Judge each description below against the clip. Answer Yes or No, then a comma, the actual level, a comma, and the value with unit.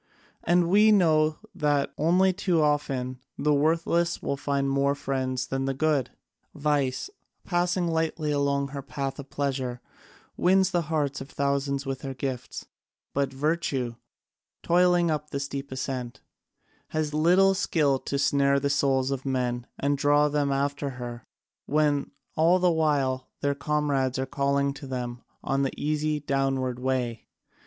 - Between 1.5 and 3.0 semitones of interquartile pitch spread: Yes, narrow, 2.4 semitones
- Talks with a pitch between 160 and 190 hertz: No, medium, 140 Hz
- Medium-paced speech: Yes, average, 145 wpm